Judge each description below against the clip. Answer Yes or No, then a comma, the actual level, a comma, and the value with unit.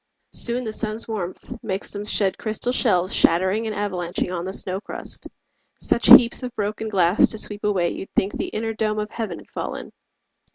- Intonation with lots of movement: No, average, 2.7 semitones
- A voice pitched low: No, high, 210 Hz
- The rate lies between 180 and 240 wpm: Yes, average, 190 wpm